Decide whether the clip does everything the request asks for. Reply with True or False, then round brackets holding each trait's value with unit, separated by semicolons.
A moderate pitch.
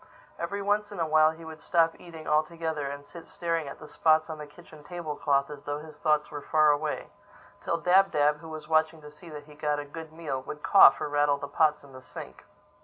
True (155 Hz)